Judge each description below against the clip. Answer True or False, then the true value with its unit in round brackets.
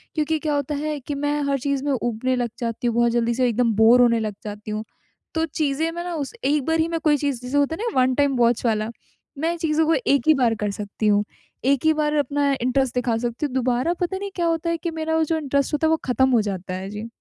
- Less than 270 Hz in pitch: False (275 Hz)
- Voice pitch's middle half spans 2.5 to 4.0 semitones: False (4.7 semitones)